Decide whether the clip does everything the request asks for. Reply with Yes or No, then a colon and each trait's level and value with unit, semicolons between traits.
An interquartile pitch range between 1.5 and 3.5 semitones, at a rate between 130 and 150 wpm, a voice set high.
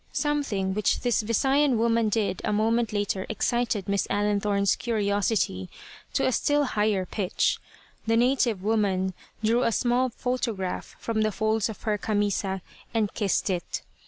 Yes: average, 2.8 semitones; average, 145 wpm; high, 215 Hz